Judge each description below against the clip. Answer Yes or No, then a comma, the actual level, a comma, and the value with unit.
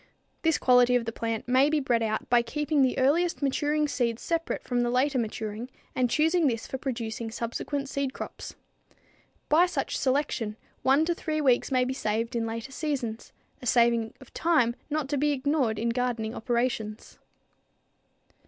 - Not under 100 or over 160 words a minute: No, average, 170 wpm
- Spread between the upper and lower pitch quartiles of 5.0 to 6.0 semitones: No, average, 3.8 semitones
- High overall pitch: Yes, very high, 255 Hz